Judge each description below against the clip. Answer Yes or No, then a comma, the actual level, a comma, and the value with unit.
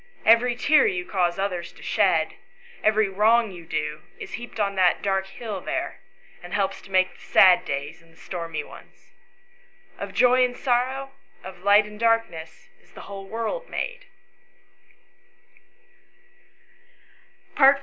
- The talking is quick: No, average, 140 wpm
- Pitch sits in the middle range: No, high, 200 Hz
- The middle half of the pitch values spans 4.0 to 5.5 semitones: Yes, average, 4.7 semitones